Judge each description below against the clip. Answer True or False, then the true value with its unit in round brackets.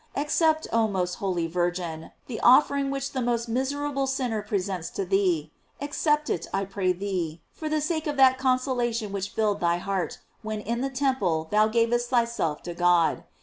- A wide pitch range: True (6.5 semitones)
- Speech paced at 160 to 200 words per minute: True (185 wpm)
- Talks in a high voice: True (220 Hz)